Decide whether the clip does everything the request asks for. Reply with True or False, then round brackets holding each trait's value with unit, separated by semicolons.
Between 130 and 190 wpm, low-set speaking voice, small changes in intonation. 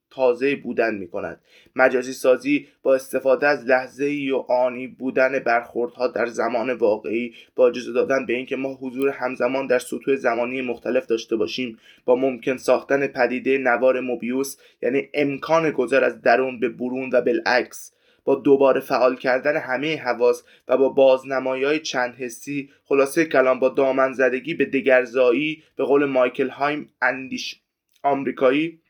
True (150 wpm; 130 Hz; 1.6 semitones)